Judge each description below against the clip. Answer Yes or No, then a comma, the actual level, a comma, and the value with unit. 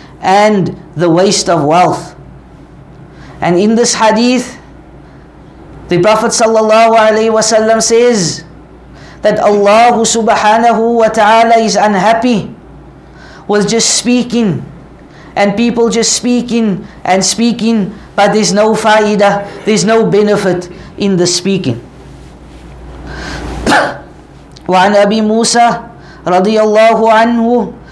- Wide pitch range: No, average, 3.7 semitones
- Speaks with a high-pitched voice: Yes, high, 210 Hz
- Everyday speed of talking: No, slow, 90 wpm